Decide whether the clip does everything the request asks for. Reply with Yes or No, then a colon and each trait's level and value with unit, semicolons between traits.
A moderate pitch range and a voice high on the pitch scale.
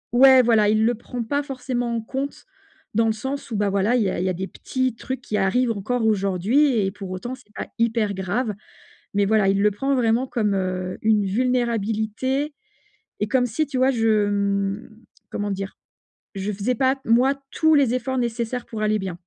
Yes: average, 3.9 semitones; high, 225 Hz